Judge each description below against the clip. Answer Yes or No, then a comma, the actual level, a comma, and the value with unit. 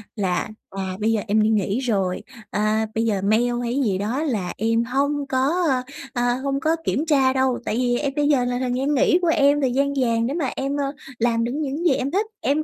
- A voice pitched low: No, very high, 255 Hz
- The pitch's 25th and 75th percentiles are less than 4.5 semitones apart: Yes, average, 3.9 semitones